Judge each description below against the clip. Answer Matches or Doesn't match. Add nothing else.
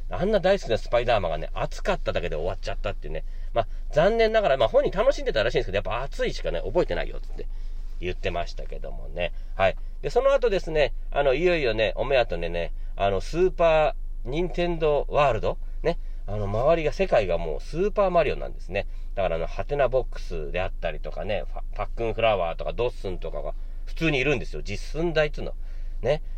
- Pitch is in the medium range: Matches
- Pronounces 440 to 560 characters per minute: Matches